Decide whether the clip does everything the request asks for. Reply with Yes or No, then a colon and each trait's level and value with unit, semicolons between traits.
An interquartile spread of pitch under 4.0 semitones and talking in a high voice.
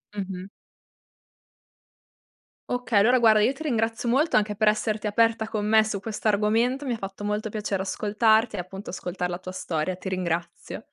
Yes: average, 2.7 semitones; high, 210 Hz